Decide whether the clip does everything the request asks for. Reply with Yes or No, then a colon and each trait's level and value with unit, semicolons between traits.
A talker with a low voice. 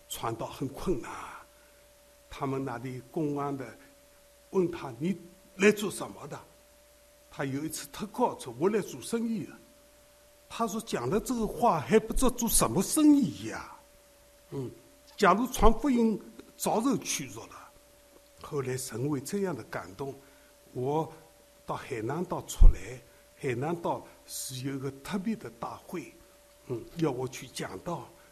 No: high, 210 Hz